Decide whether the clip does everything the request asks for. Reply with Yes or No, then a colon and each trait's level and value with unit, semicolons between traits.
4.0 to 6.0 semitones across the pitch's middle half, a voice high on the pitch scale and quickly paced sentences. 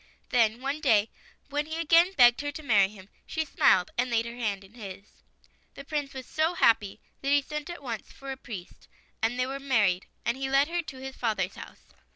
Yes: average, 4.8 semitones; very high, 260 Hz; fast, 215 wpm